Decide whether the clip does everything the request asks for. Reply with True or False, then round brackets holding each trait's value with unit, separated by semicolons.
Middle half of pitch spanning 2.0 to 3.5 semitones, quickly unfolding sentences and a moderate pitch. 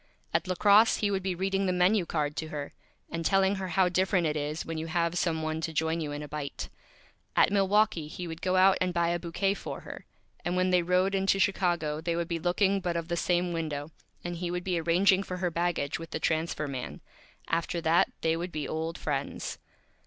True (2.5 semitones; 225 wpm; 175 Hz)